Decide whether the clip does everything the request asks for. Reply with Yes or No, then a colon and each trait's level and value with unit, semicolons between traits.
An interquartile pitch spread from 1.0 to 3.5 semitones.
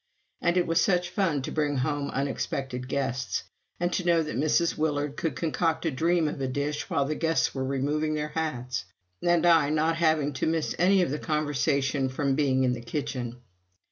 Yes: average, 3.2 semitones